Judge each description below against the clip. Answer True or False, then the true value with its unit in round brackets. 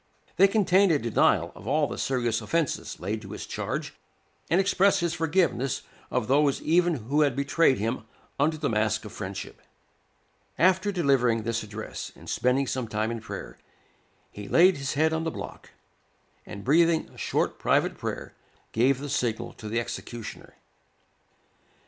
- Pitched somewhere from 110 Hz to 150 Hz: True (135 Hz)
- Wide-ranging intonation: True (6.3 semitones)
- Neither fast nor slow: True (160 wpm)